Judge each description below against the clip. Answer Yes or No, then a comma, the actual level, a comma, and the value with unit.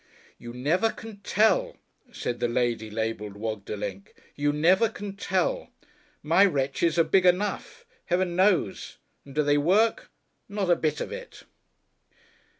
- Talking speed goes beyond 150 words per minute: No, average, 140 wpm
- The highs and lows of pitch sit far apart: Yes, wide, 8.5 semitones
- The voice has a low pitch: No, medium, 170 Hz